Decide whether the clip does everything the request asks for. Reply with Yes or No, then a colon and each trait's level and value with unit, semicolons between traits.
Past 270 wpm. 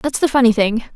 No: fast, 250 wpm